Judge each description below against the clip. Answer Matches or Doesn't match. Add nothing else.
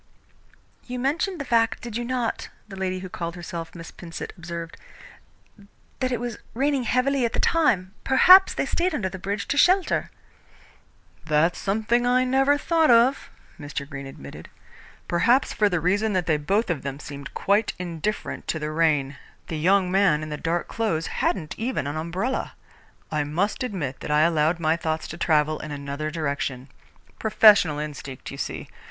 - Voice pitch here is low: Doesn't match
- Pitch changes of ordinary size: Doesn't match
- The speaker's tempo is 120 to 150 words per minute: Doesn't match